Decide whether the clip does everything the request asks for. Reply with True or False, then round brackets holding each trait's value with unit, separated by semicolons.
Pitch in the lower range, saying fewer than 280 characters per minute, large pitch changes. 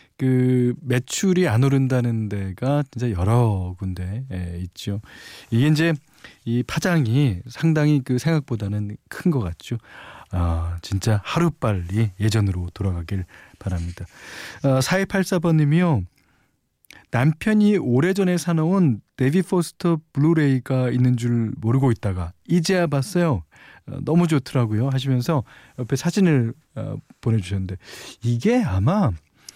True (125 Hz; 260 characters per minute; 7.1 semitones)